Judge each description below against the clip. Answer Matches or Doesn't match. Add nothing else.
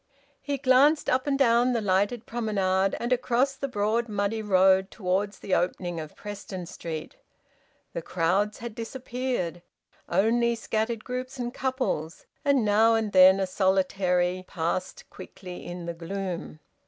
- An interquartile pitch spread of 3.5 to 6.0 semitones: Matches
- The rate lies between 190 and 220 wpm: Doesn't match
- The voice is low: Doesn't match